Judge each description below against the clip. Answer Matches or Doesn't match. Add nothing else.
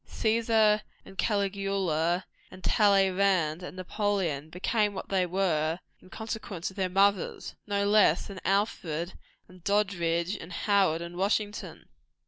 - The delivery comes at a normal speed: Doesn't match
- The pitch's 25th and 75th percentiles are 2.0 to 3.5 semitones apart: Matches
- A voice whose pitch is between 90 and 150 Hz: Doesn't match